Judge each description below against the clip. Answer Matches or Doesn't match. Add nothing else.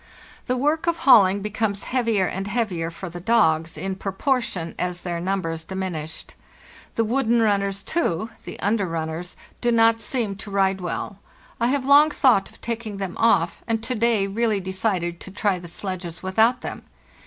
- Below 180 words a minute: Matches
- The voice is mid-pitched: Doesn't match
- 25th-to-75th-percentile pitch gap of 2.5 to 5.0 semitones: Matches